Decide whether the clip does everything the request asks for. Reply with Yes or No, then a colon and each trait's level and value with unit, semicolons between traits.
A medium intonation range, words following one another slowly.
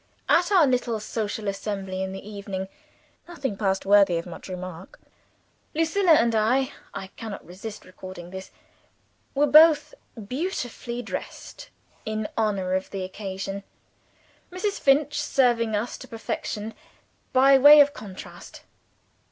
No: wide, 5.9 semitones; slow, 125 wpm